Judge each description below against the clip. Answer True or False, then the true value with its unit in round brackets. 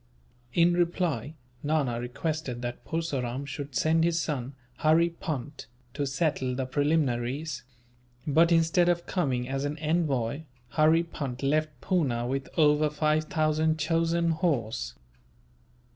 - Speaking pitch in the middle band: True (150 Hz)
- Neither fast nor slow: False (125 wpm)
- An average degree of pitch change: True (3.7 semitones)